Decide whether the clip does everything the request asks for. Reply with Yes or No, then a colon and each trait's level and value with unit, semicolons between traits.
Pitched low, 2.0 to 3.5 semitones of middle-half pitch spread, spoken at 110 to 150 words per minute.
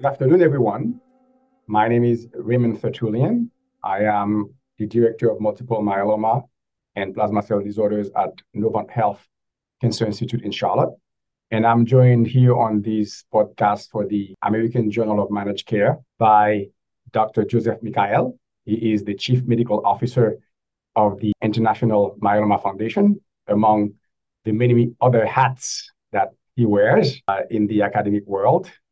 Yes: low, 110 Hz; narrow, 2.4 semitones; average, 140 wpm